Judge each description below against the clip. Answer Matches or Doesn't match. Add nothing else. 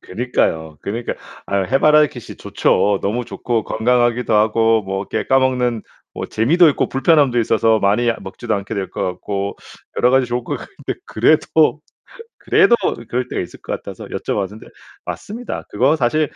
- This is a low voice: Matches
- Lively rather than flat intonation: Doesn't match